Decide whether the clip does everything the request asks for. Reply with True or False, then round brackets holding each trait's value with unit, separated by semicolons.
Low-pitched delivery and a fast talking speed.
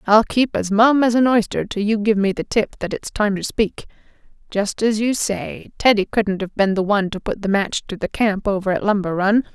False (210 Hz; 245 wpm)